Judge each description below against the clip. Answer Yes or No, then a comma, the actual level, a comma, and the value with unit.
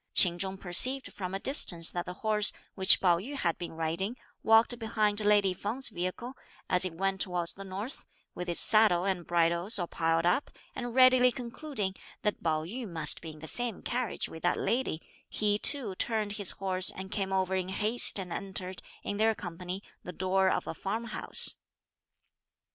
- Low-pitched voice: No, high, 190 Hz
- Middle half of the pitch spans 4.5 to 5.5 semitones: No, average, 3.8 semitones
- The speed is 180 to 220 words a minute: Yes, average, 185 wpm